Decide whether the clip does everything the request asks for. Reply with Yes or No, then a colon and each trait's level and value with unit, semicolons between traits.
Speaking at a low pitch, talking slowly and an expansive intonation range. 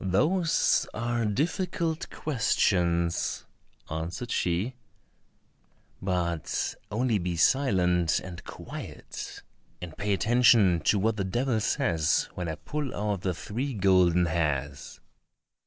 Yes: very low, 95 Hz; slow, 105 wpm; wide, 5.7 semitones